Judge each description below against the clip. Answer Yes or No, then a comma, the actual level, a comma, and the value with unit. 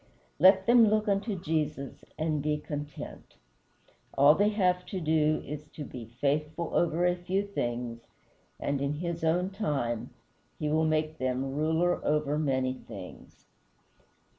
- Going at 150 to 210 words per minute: No, average, 140 wpm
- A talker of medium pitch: Yes, medium, 155 Hz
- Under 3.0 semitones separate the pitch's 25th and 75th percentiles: No, average, 3.9 semitones